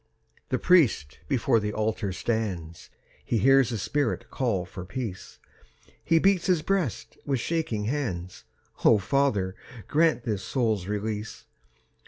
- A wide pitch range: Yes, wide, 5.7 semitones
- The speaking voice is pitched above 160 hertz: No, low, 115 Hz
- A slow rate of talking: Yes, slow, 130 wpm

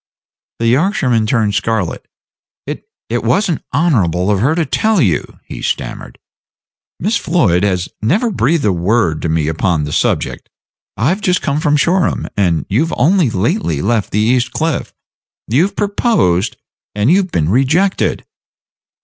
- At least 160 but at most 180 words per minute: No, average, 150 wpm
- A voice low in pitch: Yes, low, 120 Hz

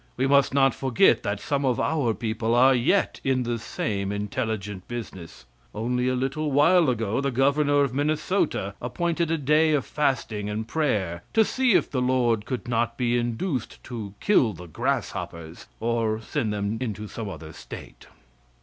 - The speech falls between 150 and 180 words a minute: Yes, average, 165 wpm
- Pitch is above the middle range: No, low, 120 Hz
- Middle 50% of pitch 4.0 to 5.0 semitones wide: Yes, average, 4.7 semitones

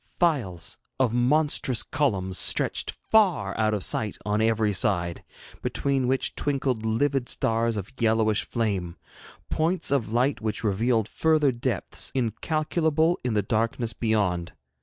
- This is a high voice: No, low, 115 Hz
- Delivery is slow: Yes, slow, 130 wpm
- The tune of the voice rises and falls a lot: No, average, 4.7 semitones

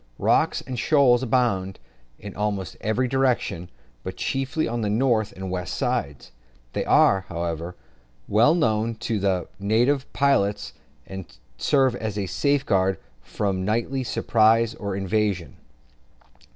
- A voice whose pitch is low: Yes, low, 110 Hz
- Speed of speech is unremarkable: No, slow, 125 wpm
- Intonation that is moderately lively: Yes, average, 4.6 semitones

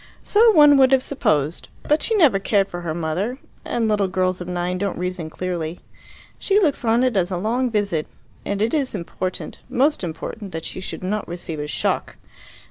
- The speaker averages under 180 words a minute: No, average, 195 wpm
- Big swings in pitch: Yes, wide, 6.2 semitones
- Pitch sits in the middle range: No, high, 195 Hz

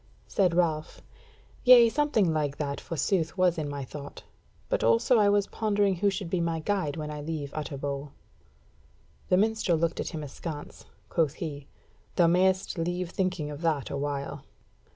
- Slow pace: No, average, 155 wpm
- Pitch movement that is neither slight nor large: Yes, average, 4.3 semitones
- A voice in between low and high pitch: Yes, medium, 165 Hz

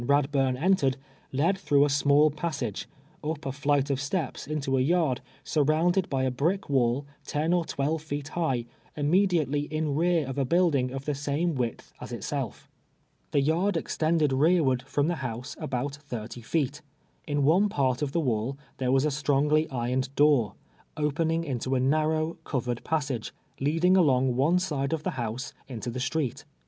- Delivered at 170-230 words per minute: Yes, average, 175 wpm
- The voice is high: No, medium, 145 Hz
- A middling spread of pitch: Yes, average, 3.3 semitones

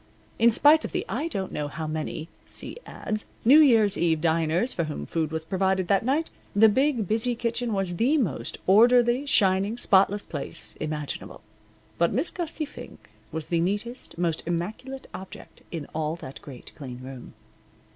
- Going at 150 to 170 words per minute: Yes, average, 165 wpm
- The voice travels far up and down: Yes, wide, 6.9 semitones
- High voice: Yes, high, 195 Hz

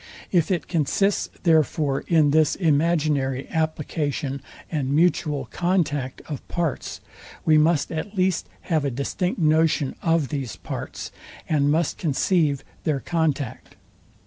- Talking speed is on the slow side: Yes, slow, 120 wpm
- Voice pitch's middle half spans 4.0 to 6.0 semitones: No, average, 2.9 semitones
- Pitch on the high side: No, medium, 155 Hz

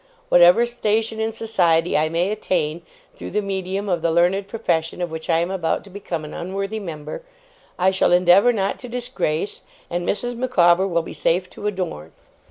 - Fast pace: No, average, 180 wpm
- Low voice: No, medium, 185 Hz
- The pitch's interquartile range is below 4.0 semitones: Yes, average, 3.5 semitones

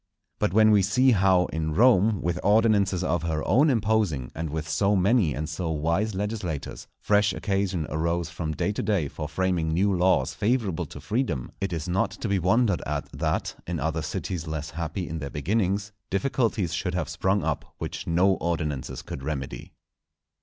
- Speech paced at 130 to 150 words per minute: No, average, 180 wpm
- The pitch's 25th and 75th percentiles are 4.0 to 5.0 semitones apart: Yes, average, 4.3 semitones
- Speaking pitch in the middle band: No, very low, 90 Hz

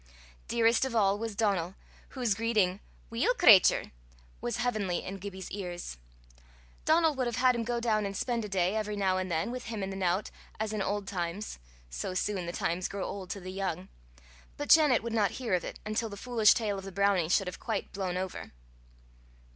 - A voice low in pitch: No, high, 205 Hz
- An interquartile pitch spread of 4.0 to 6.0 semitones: No, average, 3.6 semitones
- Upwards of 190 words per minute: Yes, average, 200 wpm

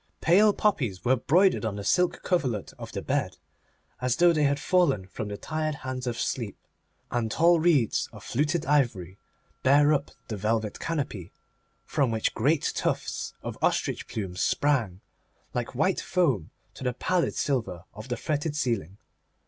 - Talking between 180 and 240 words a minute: No, average, 160 wpm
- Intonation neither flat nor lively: No, wide, 6.2 semitones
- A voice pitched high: No, low, 130 Hz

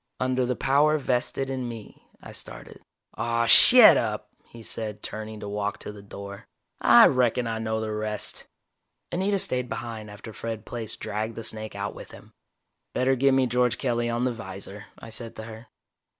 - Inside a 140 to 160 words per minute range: No, average, 185 wpm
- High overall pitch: No, low, 115 Hz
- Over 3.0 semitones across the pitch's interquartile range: No, average, 2.7 semitones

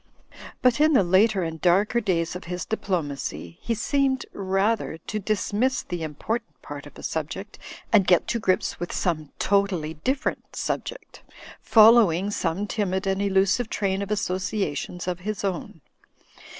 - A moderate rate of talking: Yes, average, 150 wpm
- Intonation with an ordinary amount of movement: Yes, average, 3.7 semitones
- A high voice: Yes, high, 195 Hz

